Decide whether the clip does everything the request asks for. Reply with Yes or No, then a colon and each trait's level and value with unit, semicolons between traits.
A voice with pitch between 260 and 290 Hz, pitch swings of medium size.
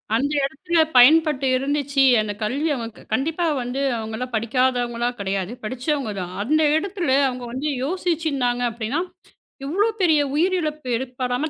Yes: very high, 265 Hz; average, 4.2 semitones